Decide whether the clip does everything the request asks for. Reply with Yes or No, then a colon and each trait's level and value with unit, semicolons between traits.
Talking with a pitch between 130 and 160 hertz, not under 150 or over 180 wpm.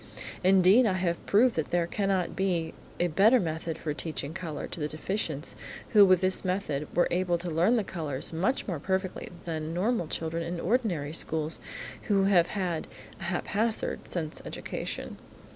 No: medium, 175 Hz; average, 170 wpm